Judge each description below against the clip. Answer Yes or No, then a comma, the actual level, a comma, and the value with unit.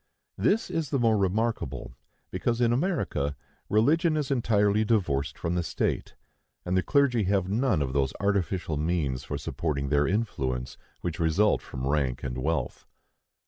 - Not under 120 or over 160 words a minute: Yes, average, 150 wpm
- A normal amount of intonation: No, wide, 8.4 semitones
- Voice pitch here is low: Yes, very low, 95 Hz